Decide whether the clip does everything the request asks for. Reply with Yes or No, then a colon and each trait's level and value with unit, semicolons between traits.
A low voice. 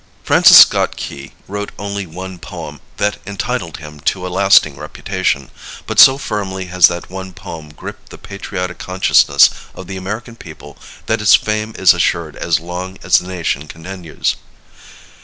Yes: very low, 95 Hz